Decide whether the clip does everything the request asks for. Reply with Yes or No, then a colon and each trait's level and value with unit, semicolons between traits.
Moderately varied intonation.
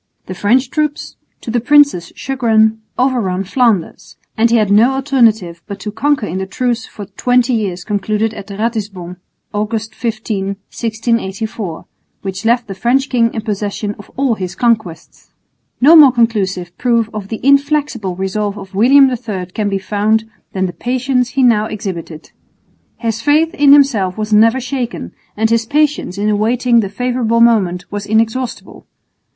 Yes: average, 3.7 semitones